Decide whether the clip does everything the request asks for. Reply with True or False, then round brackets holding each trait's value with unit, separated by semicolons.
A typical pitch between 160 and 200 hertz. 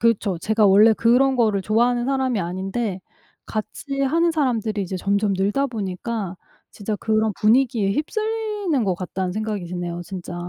False (215 Hz)